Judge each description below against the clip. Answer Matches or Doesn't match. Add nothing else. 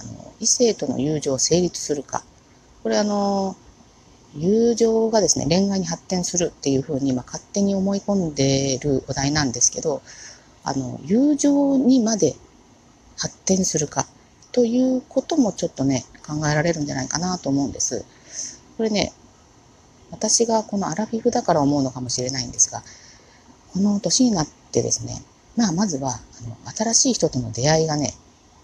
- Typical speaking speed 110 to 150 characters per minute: Doesn't match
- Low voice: Doesn't match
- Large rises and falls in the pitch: Matches